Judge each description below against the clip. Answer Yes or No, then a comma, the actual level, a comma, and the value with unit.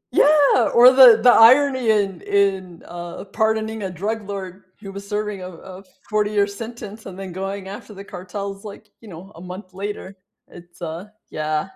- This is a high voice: Yes, high, 200 Hz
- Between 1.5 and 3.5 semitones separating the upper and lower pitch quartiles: Yes, average, 2.7 semitones